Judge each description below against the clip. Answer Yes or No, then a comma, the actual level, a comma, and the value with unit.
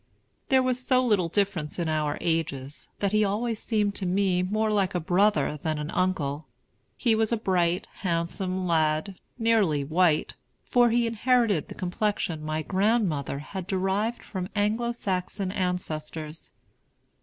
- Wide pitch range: No, average, 4.8 semitones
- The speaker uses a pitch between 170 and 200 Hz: Yes, medium, 185 Hz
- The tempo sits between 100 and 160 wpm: Yes, average, 145 wpm